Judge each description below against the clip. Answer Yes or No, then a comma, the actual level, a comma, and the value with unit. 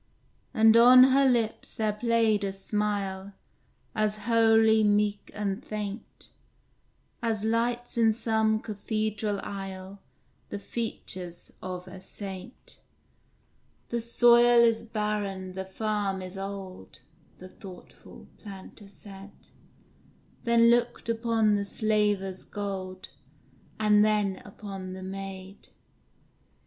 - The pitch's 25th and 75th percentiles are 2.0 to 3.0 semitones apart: Yes, narrow, 2.5 semitones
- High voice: Yes, high, 210 Hz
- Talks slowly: Yes, slow, 105 wpm